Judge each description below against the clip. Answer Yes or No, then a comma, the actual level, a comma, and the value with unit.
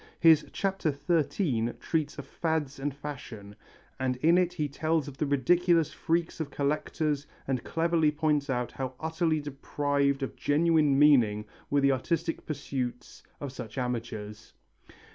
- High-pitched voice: No, medium, 145 Hz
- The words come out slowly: No, average, 145 wpm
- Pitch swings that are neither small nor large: Yes, average, 3.4 semitones